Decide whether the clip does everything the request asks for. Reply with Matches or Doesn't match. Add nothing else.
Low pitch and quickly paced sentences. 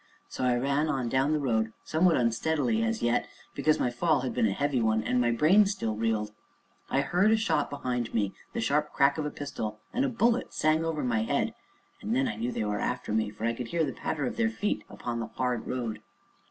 Matches